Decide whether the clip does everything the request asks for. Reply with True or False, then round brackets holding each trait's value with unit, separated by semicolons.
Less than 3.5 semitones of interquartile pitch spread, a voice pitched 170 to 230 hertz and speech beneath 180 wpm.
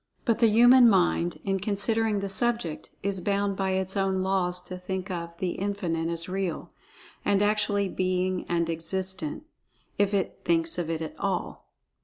True (2.6 semitones; 190 Hz; 165 wpm)